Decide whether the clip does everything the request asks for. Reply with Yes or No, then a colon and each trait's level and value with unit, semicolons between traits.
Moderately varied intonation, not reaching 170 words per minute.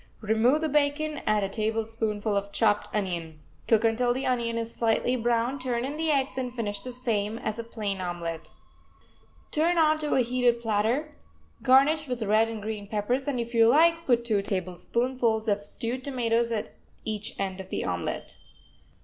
No: average, 3.5 semitones; average, 175 wpm